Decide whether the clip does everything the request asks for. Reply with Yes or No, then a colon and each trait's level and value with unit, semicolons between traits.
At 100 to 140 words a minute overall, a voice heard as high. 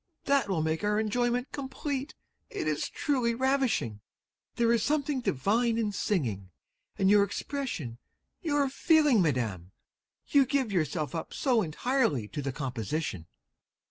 Yes: slow, 135 wpm; high, 220 Hz